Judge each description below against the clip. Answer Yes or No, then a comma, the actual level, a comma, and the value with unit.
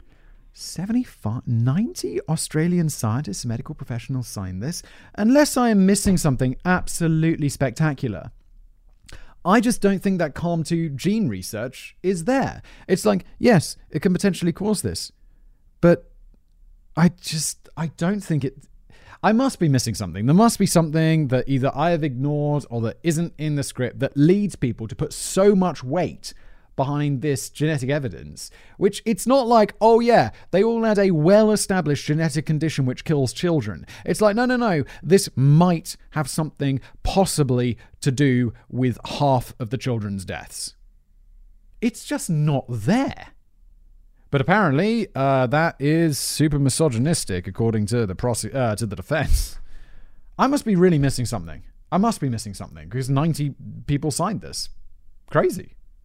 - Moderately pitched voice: Yes, medium, 150 Hz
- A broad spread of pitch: Yes, wide, 7.0 semitones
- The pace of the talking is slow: No, average, 155 wpm